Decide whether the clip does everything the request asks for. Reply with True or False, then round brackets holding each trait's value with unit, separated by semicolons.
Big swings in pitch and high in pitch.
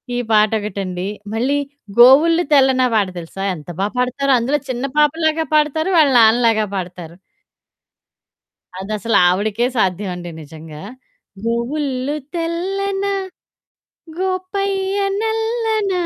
True (8.3 semitones; 255 Hz)